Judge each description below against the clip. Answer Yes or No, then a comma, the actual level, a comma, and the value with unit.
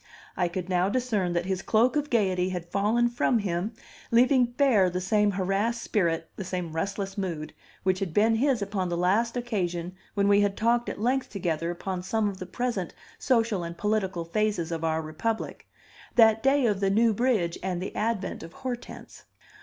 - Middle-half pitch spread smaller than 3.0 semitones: No, average, 4.3 semitones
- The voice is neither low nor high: No, high, 200 Hz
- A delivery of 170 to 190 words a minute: Yes, average, 185 wpm